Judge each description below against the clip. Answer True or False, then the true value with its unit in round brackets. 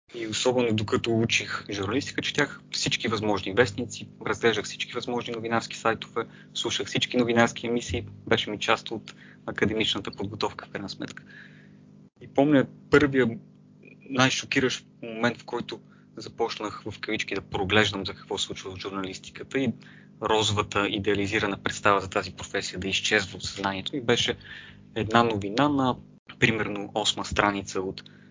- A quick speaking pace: False (135 wpm)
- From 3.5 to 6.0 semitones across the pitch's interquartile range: False (3.0 semitones)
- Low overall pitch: True (110 Hz)